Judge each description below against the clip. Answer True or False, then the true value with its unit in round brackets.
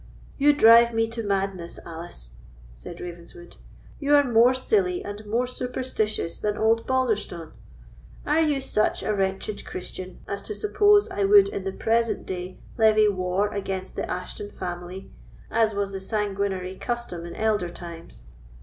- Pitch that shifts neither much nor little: True (4.0 semitones)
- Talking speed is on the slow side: False (150 wpm)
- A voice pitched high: True (205 Hz)